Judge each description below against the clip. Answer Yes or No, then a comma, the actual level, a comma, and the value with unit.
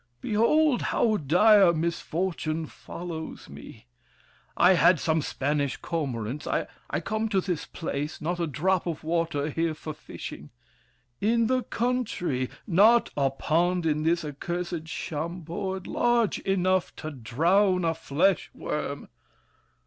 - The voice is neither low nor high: Yes, medium, 170 Hz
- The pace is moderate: No, slow, 120 wpm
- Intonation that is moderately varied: Yes, average, 3.8 semitones